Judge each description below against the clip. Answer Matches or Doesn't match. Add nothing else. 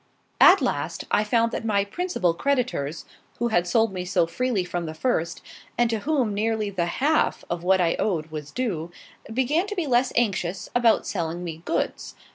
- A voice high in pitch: Matches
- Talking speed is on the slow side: Doesn't match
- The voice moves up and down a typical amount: Doesn't match